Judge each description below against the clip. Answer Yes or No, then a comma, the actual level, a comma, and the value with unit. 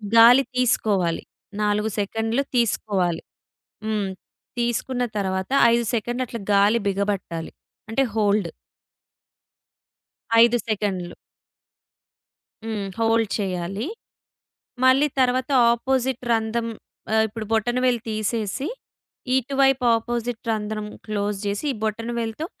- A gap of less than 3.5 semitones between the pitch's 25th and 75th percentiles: Yes, average, 2.9 semitones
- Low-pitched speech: No, high, 225 Hz